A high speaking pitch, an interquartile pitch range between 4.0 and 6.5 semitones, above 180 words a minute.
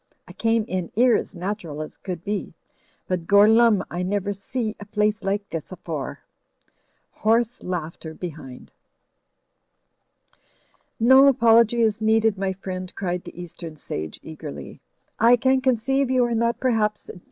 No: high, 205 Hz; average, 4.4 semitones; average, 145 wpm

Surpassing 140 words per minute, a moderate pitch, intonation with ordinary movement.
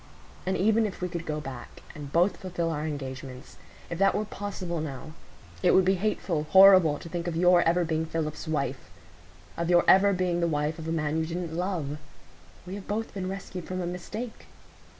Yes: average, 190 wpm; medium, 170 Hz; average, 3.5 semitones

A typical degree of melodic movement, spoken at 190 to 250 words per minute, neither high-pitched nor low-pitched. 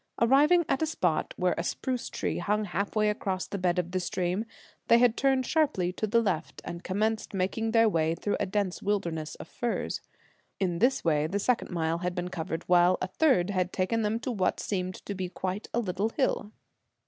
No: average, 4.0 semitones; fast, 205 wpm; high, 195 Hz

